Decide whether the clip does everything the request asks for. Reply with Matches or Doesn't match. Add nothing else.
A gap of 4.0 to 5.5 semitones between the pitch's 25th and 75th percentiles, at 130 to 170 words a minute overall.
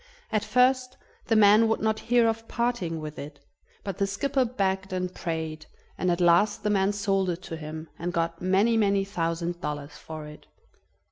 Doesn't match